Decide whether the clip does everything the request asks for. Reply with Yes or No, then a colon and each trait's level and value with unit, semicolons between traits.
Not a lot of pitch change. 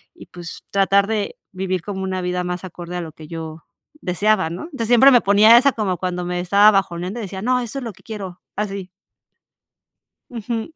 No: average, 3.3 semitones